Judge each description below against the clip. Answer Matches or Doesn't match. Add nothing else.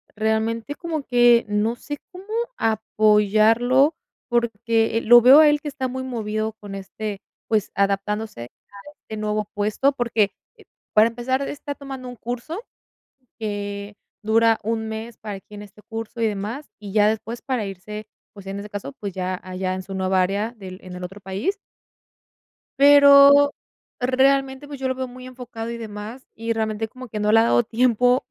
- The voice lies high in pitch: Matches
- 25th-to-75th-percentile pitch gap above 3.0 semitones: Matches